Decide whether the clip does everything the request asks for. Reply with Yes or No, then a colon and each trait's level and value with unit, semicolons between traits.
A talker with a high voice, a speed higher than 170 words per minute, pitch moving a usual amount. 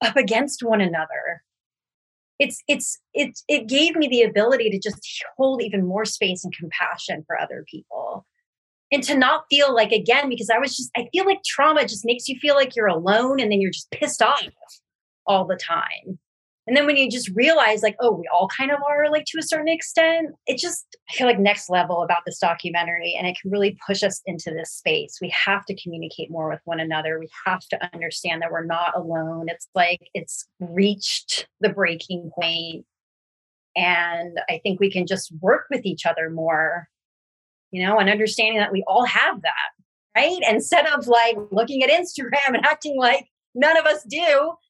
No: high, 215 Hz; average, 195 wpm; wide, 8.0 semitones